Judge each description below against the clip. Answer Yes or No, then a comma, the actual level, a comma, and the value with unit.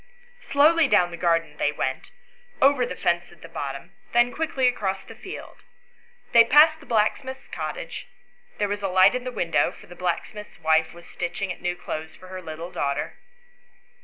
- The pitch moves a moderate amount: No, wide, 6.7 semitones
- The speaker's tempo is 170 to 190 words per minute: Yes, average, 180 wpm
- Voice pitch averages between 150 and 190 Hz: Yes, medium, 185 Hz